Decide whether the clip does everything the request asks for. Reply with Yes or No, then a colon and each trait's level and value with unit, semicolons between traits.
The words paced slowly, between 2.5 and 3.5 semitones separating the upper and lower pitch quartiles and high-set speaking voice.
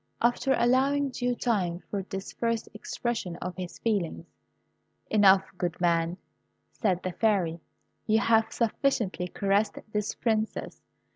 No: slow, 125 wpm; average, 4.2 semitones; high, 210 Hz